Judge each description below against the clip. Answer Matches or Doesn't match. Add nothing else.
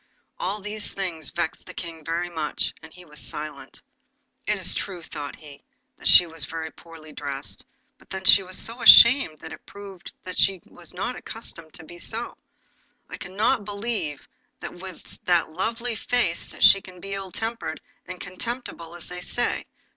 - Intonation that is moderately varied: Matches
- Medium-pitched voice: Matches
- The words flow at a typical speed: Matches